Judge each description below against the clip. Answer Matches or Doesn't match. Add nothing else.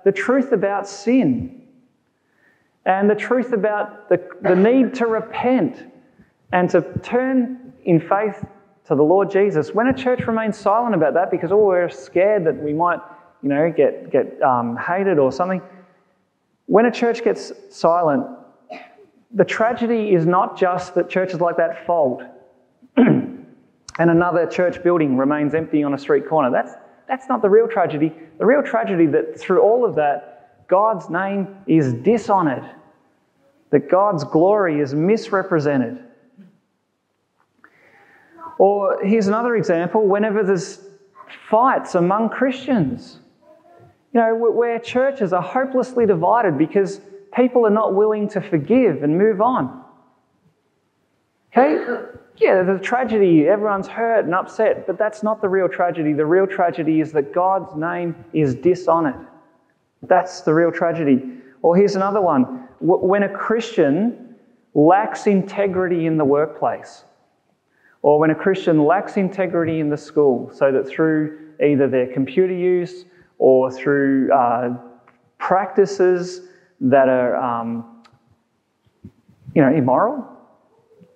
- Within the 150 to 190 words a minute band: Doesn't match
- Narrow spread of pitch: Doesn't match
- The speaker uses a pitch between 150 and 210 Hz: Matches